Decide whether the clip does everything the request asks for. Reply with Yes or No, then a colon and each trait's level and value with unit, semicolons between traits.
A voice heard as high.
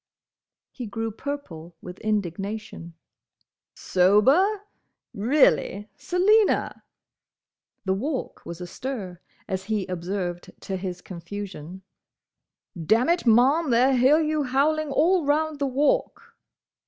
Yes: high, 225 Hz